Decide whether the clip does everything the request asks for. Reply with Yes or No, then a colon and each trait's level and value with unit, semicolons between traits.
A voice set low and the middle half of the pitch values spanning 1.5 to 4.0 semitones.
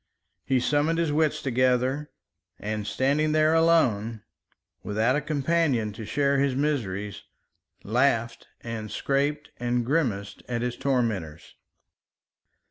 No: low, 130 Hz; average, 4.7 semitones